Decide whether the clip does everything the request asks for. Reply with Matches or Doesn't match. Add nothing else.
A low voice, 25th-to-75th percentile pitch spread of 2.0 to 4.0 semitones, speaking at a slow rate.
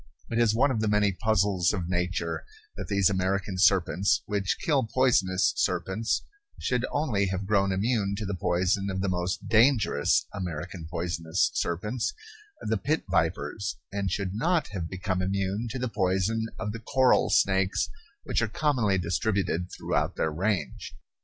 Doesn't match